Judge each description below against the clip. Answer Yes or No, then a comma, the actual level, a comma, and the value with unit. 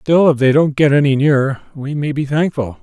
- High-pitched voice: No, medium, 145 Hz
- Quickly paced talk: Yes, fast, 235 wpm